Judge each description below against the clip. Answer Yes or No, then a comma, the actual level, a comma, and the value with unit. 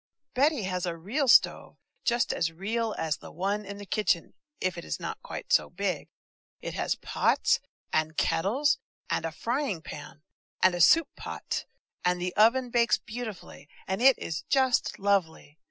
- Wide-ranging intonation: Yes, wide, 5.9 semitones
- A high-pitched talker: Yes, high, 195 Hz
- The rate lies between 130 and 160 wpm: No, average, 170 wpm